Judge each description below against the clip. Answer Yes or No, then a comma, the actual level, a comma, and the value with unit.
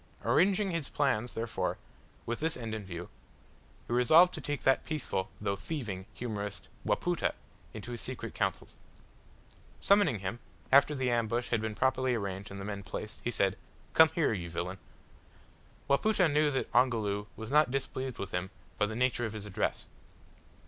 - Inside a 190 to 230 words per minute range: No, average, 165 wpm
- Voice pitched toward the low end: Yes, low, 120 Hz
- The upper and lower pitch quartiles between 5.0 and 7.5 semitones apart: Yes, wide, 5.5 semitones